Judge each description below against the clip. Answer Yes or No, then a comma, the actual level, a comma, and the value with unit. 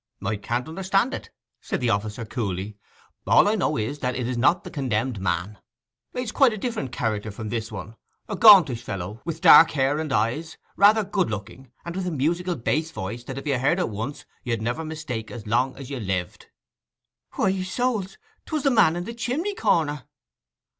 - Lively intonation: Yes, wide, 8.5 semitones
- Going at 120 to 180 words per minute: No, average, 190 wpm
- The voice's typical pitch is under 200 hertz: Yes, low, 135 Hz